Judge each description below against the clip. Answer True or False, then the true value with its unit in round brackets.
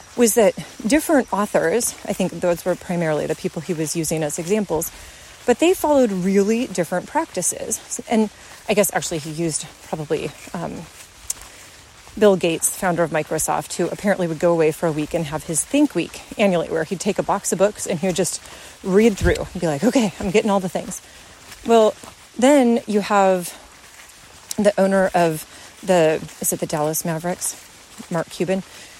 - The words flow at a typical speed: True (175 wpm)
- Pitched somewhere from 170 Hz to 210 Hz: True (190 Hz)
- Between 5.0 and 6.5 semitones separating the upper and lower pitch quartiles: False (4.2 semitones)